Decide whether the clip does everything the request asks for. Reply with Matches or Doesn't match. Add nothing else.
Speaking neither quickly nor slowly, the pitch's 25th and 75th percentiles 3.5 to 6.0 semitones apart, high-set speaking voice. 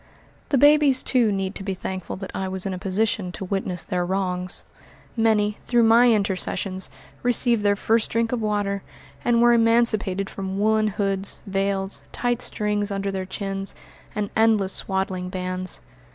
Doesn't match